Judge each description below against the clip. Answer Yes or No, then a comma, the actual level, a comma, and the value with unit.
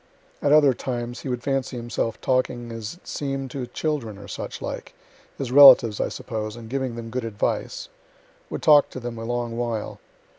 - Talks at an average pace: Yes, average, 185 wpm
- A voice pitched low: Yes, low, 120 Hz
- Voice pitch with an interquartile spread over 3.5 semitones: No, average, 2.7 semitones